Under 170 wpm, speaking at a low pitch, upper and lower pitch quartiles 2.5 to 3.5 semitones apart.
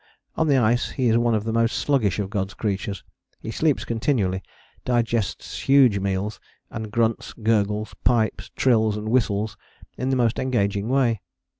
Yes: average, 160 wpm; low, 115 Hz; average, 2.9 semitones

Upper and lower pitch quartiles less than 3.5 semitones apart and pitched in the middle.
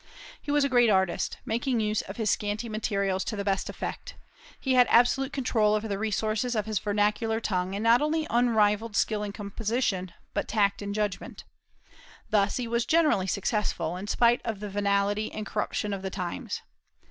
No: average, 2.7 semitones; high, 215 Hz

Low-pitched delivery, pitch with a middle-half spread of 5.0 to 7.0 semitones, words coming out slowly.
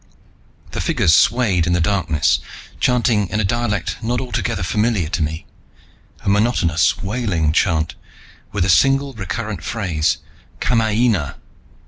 Yes: low, 100 Hz; wide, 5.5 semitones; slow, 125 wpm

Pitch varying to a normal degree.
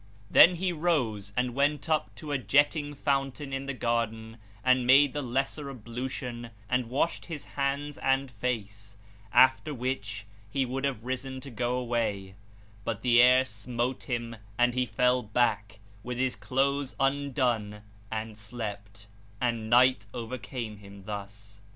Yes: average, 3.5 semitones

